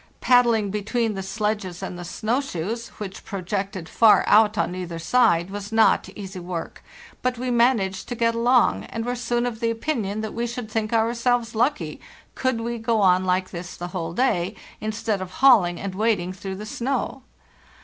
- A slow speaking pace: No, average, 180 wpm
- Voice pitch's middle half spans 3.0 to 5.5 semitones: Yes, average, 3.9 semitones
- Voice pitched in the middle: No, high, 215 Hz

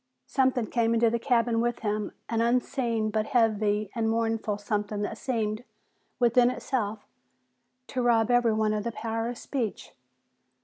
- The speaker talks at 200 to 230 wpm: No, average, 145 wpm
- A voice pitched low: No, high, 225 Hz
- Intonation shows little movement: Yes, narrow, 1.9 semitones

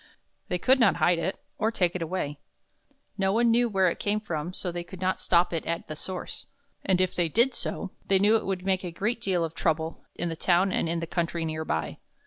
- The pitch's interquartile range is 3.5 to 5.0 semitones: No, average, 2.7 semitones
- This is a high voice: No, medium, 180 Hz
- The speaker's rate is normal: No, fast, 250 wpm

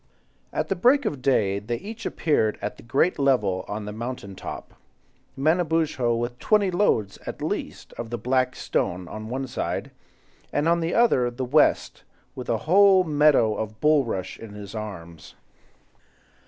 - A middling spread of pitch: No, wide, 6.6 semitones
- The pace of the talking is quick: No, average, 160 wpm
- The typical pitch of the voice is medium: No, low, 125 Hz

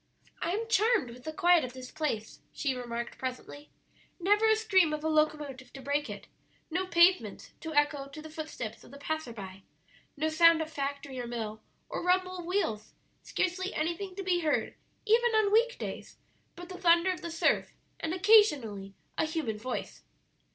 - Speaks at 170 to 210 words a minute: Yes, average, 180 wpm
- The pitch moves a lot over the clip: Yes, wide, 5.9 semitones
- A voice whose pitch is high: Yes, very high, 315 Hz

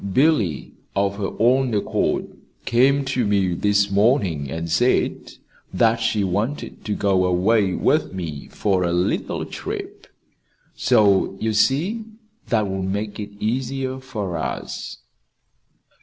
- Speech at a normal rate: No, slow, 125 wpm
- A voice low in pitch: Yes, low, 105 Hz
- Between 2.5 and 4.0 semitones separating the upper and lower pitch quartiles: No, average, 4.5 semitones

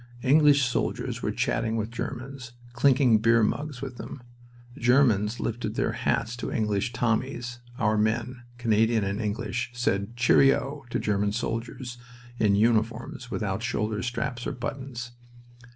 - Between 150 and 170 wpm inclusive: No, slow, 135 wpm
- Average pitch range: No, narrow, 2.3 semitones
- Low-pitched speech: Yes, low, 120 Hz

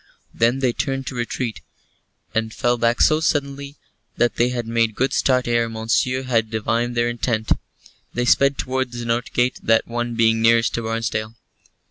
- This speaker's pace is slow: No, average, 170 wpm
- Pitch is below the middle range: Yes, low, 120 Hz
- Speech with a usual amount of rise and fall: No, narrow, 1.9 semitones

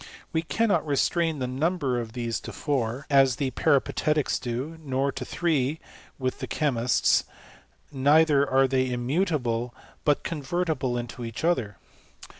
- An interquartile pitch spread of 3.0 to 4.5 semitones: Yes, average, 4.0 semitones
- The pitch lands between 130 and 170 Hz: Yes, low, 135 Hz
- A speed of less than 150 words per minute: Yes, slow, 135 wpm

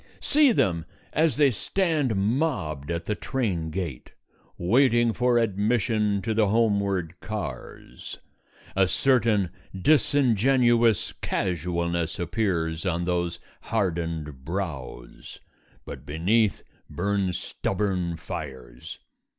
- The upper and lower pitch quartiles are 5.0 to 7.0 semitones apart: Yes, wide, 5.5 semitones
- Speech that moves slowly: Yes, slow, 95 wpm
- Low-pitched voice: Yes, very low, 95 Hz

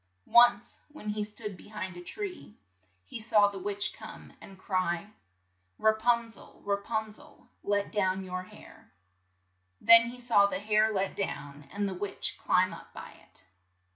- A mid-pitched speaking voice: No, high, 205 Hz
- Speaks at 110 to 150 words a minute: No, average, 175 wpm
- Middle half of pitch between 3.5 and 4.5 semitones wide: No, average, 2.7 semitones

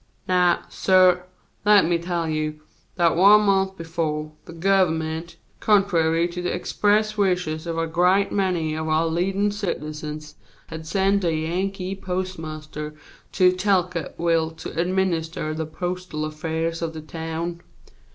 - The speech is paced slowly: Yes, slow, 130 wpm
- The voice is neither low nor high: Yes, medium, 170 Hz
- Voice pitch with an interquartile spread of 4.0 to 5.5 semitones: No, average, 2.8 semitones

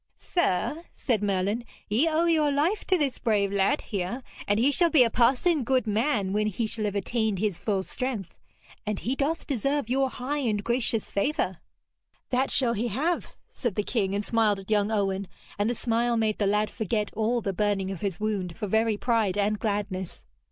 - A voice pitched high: Yes, high, 220 Hz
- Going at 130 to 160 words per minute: No, average, 195 wpm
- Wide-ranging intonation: No, average, 4.0 semitones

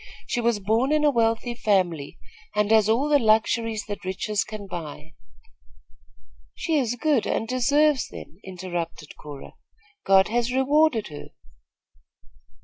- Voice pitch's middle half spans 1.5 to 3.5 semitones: No, average, 4.9 semitones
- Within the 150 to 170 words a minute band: No, average, 140 wpm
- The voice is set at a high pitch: Yes, high, 220 Hz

